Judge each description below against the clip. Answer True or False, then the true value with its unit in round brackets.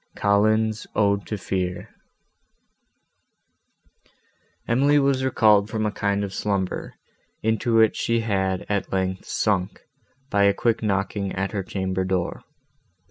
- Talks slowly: True (125 wpm)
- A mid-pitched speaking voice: False (100 Hz)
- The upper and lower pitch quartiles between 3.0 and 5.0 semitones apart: False (2.5 semitones)